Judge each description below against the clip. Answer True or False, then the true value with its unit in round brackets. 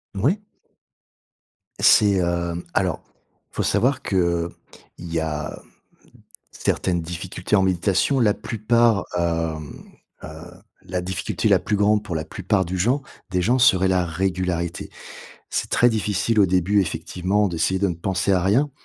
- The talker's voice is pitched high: False (95 Hz)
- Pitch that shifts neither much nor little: True (3.2 semitones)